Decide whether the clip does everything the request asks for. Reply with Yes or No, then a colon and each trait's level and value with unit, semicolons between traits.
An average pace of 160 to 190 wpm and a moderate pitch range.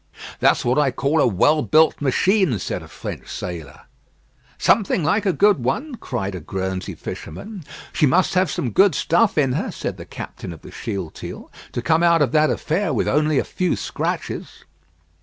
No: average, 180 wpm; wide, 7.0 semitones